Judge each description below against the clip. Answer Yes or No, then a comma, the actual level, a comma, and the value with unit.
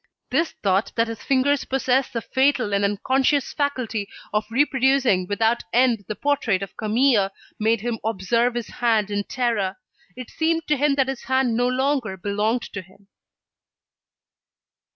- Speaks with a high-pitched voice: Yes, high, 235 Hz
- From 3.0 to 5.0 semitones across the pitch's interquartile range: Yes, average, 4.3 semitones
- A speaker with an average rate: Yes, average, 150 wpm